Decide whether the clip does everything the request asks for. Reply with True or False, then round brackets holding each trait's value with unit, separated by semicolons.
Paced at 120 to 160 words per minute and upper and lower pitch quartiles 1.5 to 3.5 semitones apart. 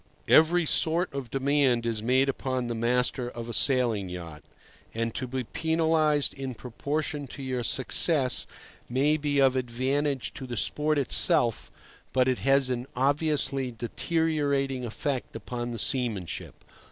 True (140 wpm; 3.1 semitones)